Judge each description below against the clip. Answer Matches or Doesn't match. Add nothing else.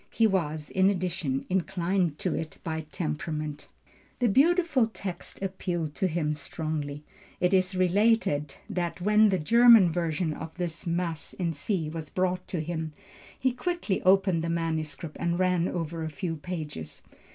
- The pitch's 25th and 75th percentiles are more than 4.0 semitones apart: Doesn't match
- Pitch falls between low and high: Matches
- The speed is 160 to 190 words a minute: Doesn't match